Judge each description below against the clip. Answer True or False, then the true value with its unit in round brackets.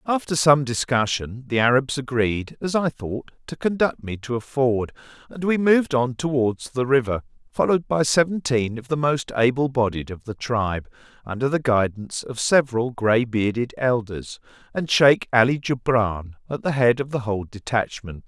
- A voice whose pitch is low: True (125 Hz)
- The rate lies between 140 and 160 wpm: False (170 wpm)